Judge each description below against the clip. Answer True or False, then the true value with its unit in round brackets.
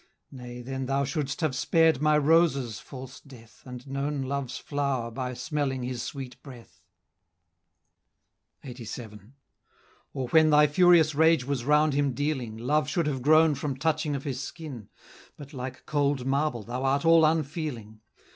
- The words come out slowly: False (150 wpm)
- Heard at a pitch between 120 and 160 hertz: True (140 Hz)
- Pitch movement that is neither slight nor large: True (3.1 semitones)